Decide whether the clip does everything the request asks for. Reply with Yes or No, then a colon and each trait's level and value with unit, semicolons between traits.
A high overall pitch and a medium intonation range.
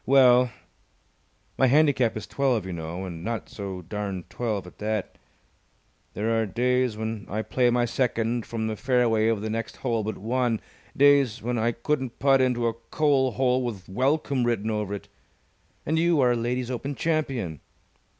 No: low, 120 Hz; average, 3.1 semitones